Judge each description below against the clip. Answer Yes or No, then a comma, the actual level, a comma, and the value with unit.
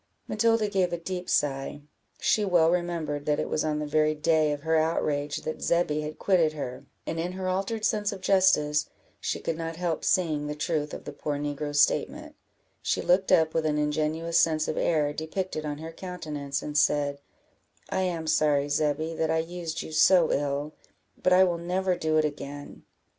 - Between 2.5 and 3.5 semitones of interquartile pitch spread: Yes, average, 3.0 semitones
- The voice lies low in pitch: No, medium, 160 Hz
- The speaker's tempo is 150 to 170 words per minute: No, average, 190 wpm